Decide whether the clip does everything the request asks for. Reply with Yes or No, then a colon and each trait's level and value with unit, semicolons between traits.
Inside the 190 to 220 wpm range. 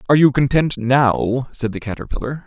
No: average, 170 wpm